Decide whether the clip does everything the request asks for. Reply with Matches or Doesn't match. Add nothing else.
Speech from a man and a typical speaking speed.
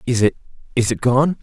Matches